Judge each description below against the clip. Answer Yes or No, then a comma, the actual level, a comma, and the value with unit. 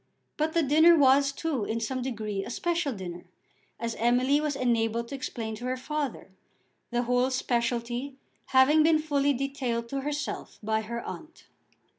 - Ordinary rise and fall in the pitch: Yes, average, 3.6 semitones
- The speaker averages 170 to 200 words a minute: No, average, 160 wpm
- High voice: Yes, very high, 255 Hz